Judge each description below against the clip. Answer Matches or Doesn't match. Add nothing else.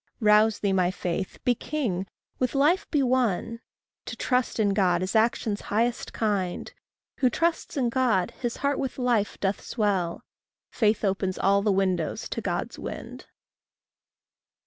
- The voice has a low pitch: Doesn't match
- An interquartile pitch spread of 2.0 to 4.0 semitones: Doesn't match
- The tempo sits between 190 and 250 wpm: Doesn't match